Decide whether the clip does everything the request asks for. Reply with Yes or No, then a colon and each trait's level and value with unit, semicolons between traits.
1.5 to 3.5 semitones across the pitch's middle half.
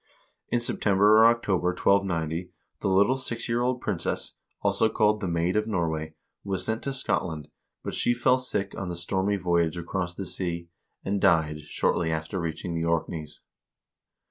No: average, 4.2 semitones